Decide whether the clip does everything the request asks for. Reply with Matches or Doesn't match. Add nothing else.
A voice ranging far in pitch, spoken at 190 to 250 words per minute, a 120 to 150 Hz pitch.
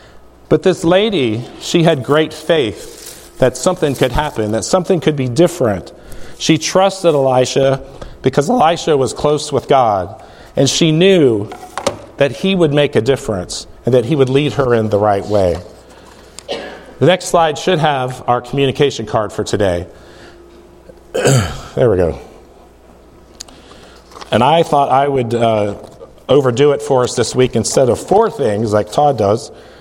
Doesn't match